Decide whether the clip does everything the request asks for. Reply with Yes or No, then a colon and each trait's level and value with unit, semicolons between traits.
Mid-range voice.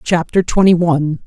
Yes: medium, 170 Hz